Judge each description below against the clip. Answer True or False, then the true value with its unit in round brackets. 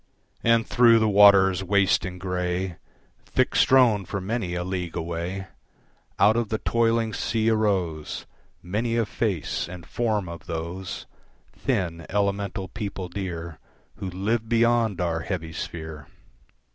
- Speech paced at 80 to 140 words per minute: True (135 wpm)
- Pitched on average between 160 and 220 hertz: False (95 Hz)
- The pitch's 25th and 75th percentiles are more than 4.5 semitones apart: False (3.9 semitones)